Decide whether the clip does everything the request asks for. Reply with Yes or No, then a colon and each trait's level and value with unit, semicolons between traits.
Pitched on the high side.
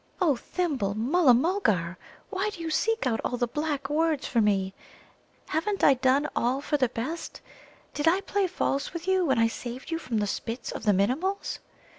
Yes: very high, 280 Hz